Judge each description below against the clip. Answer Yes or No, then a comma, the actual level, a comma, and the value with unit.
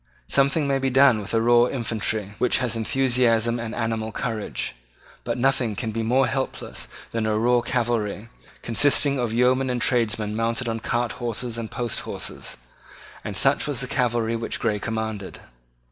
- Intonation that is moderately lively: No, narrow, 2.1 semitones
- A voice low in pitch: Yes, low, 115 Hz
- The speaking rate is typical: Yes, average, 165 wpm